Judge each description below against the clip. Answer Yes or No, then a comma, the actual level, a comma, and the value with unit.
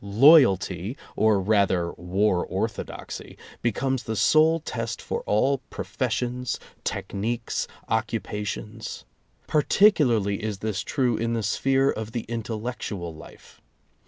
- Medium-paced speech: No, slow, 110 wpm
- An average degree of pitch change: Yes, average, 3.7 semitones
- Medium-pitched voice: No, low, 110 Hz